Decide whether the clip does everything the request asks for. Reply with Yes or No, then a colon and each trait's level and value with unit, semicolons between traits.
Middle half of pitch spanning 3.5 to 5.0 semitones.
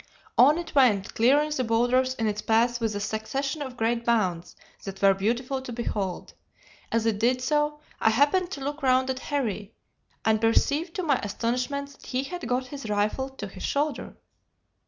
Yes: average, 4.1 semitones